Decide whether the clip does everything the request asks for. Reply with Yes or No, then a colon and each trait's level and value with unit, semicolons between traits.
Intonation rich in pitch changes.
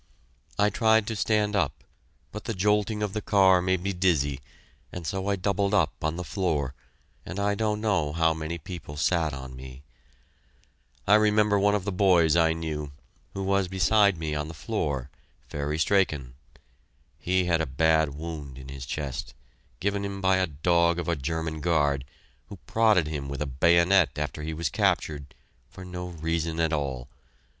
No: average, 4.6 semitones